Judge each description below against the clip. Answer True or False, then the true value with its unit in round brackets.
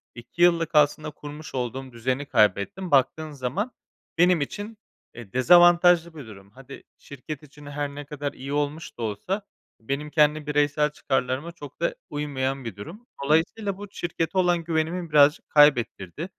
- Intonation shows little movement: False (4.0 semitones)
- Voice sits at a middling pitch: True (150 Hz)